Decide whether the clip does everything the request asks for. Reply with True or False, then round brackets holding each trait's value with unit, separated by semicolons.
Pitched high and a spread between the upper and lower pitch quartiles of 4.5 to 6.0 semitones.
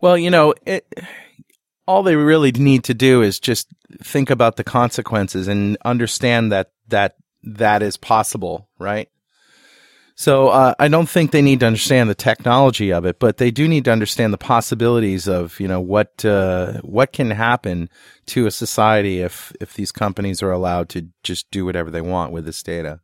False (110 Hz; 5.0 semitones)